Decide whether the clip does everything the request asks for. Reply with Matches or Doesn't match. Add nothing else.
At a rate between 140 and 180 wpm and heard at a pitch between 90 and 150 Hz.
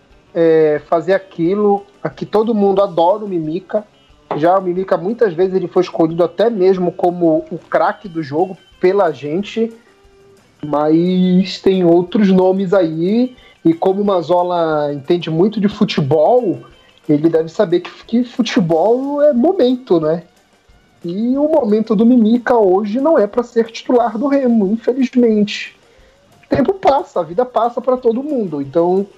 Doesn't match